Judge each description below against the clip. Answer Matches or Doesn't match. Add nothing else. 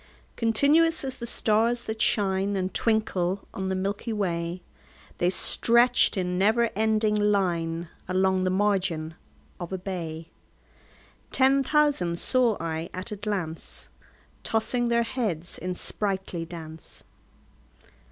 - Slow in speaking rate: Matches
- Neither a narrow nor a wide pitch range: Matches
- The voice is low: Doesn't match